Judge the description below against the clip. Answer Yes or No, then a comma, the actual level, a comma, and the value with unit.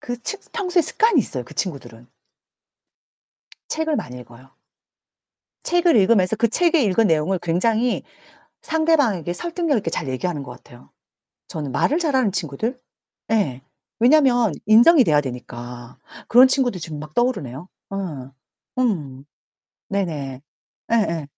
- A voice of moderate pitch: No, high, 195 Hz